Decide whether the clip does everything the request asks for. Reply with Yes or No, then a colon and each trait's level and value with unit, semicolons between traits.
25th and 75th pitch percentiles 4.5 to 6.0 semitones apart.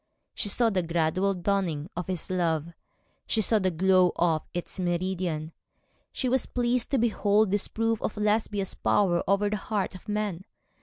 No: average, 3.3 semitones